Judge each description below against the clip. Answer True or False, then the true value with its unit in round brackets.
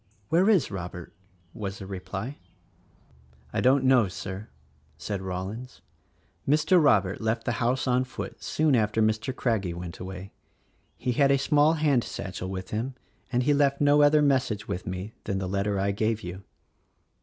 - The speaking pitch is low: True (110 Hz)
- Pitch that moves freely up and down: True (6.0 semitones)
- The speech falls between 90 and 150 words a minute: False (170 wpm)